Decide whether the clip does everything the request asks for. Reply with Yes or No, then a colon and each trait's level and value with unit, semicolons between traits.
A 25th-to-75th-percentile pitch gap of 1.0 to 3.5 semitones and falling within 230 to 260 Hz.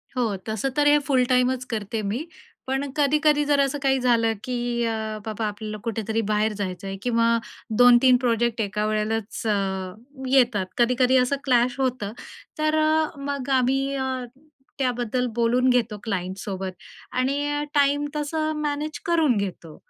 No: average, 4.1 semitones; very high, 250 Hz